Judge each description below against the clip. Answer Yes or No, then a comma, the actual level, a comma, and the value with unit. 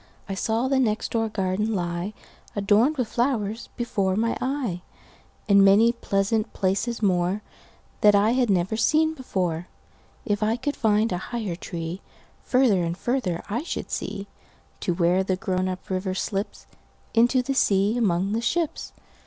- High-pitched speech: Yes, high, 210 Hz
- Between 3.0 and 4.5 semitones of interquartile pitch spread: Yes, average, 4.0 semitones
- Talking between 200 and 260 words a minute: No, slow, 135 wpm